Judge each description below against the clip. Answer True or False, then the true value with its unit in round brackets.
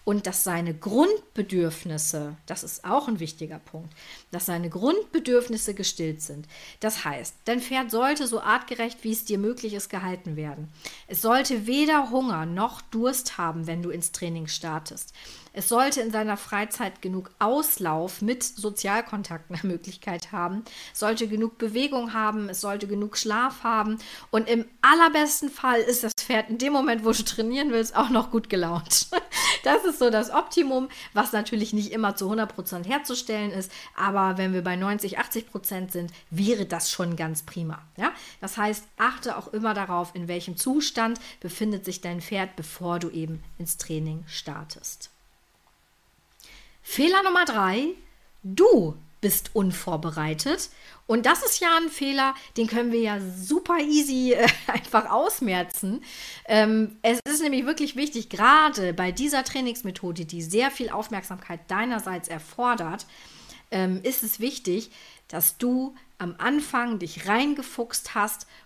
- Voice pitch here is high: True (215 Hz)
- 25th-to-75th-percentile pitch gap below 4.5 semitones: False (5.4 semitones)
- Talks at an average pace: True (150 wpm)